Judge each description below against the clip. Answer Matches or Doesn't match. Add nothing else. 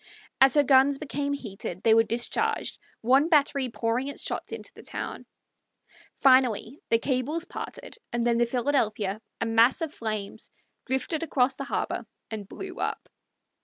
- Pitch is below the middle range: Doesn't match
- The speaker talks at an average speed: Matches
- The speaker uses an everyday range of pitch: Matches